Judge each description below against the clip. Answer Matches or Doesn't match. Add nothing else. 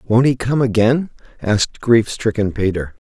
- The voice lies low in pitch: Matches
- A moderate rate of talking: Matches